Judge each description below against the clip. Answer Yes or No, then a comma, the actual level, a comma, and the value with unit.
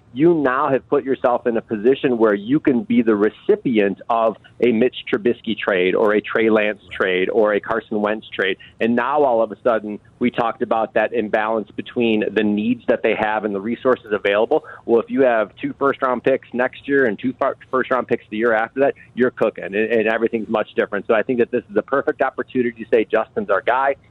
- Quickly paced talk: Yes, fast, 220 wpm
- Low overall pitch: Yes, low, 115 Hz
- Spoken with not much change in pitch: No, average, 3.1 semitones